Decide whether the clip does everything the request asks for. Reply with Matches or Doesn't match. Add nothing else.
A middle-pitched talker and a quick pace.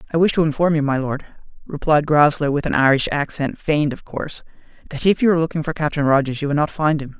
Matches